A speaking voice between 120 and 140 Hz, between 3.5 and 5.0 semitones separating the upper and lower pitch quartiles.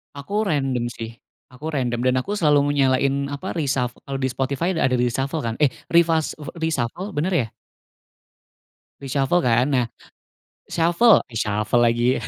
Yes: low, 135 Hz; average, 4.4 semitones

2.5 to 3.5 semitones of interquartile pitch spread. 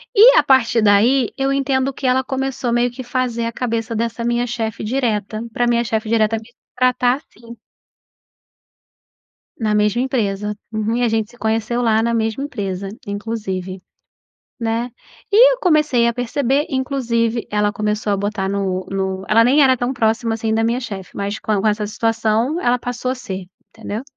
Yes: average, 2.8 semitones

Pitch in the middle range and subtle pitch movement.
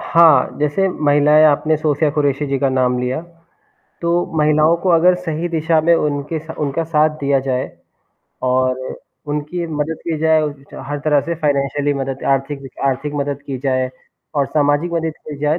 Yes: medium, 150 Hz; narrow, 2.3 semitones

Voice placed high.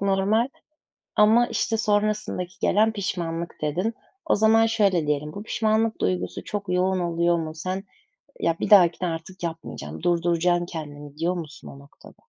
No: medium, 180 Hz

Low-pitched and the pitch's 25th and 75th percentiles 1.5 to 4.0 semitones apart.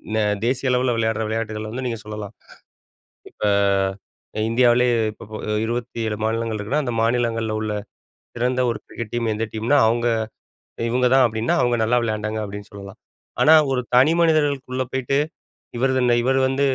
Yes: low, 120 Hz; narrow, 2.5 semitones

